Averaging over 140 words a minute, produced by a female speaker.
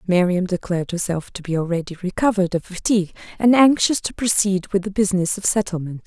Yes: average, 180 wpm; female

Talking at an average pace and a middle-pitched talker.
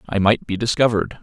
No: average, 195 wpm; low, 110 Hz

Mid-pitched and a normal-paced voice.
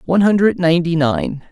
Yes: medium, 170 Hz; average, 160 wpm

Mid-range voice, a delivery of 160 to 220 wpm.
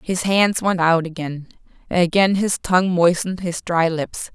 No: medium, 175 Hz; average, 150 wpm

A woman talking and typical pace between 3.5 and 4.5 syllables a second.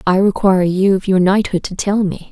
No: female; 5.5 syllables/s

